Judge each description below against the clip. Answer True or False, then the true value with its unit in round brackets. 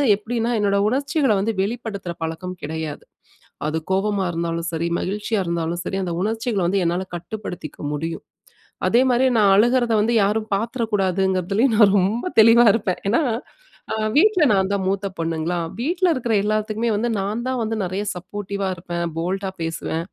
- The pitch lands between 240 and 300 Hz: False (200 Hz)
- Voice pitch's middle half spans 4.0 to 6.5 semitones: True (4.4 semitones)